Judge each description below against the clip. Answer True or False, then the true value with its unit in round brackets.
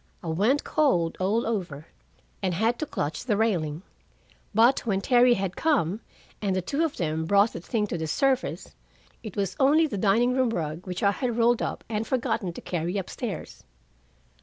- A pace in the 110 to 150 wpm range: False (185 wpm)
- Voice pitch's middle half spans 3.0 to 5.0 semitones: False (5.4 semitones)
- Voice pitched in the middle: False (210 Hz)